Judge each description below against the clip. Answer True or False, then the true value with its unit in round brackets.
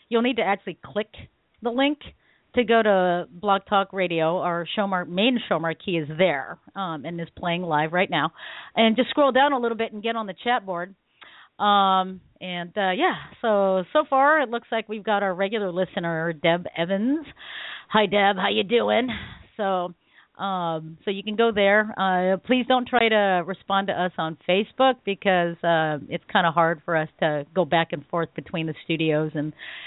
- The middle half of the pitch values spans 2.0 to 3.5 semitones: False (4.3 semitones)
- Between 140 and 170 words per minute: False (195 wpm)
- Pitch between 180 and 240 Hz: True (190 Hz)